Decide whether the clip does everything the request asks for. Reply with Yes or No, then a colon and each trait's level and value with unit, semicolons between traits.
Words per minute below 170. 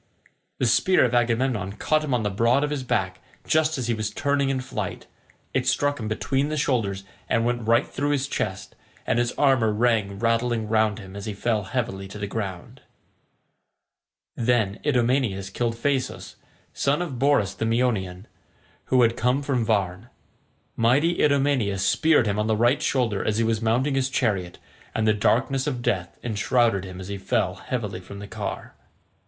No: average, 180 wpm